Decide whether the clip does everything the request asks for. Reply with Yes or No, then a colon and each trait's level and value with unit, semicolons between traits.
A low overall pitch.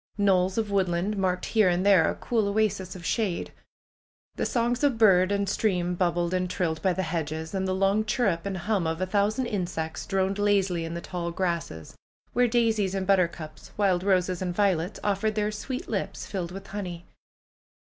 No: high, 190 Hz